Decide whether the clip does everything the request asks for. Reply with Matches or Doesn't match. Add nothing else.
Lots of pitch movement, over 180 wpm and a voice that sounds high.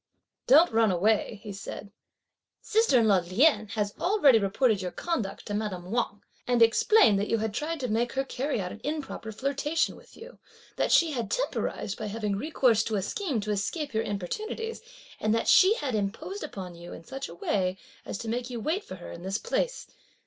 Matches